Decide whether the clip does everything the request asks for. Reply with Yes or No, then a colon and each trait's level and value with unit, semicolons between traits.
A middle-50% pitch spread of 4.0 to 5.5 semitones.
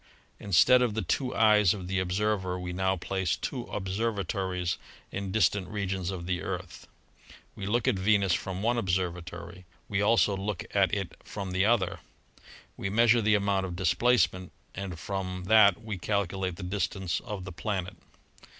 No: narrow, 2.4 semitones